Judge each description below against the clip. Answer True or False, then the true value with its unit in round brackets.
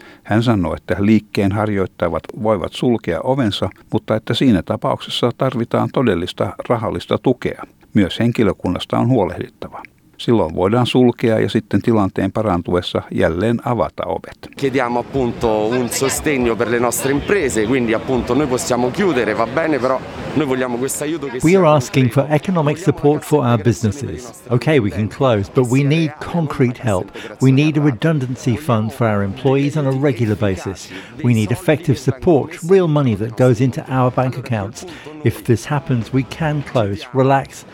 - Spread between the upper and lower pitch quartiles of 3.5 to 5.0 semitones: True (3.9 semitones)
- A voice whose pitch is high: False (125 Hz)